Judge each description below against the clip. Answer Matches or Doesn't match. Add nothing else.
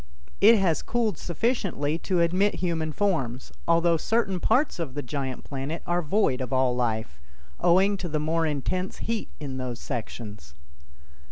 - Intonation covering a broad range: Matches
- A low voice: Doesn't match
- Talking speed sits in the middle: Matches